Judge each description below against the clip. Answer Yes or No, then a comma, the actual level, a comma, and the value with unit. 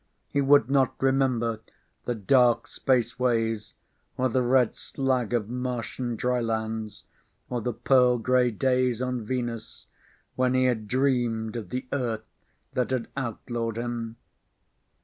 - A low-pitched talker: Yes, low, 120 Hz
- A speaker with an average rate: No, slow, 130 wpm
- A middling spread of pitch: No, narrow, 2.0 semitones